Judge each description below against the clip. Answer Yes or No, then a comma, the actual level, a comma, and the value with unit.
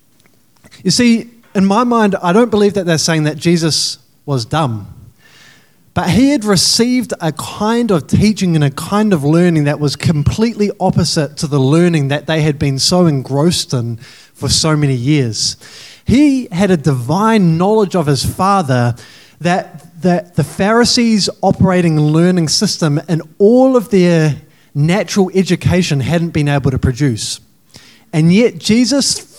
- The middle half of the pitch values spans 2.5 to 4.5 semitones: No, average, 5.3 semitones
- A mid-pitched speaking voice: Yes, medium, 170 Hz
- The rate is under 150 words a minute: No, average, 155 wpm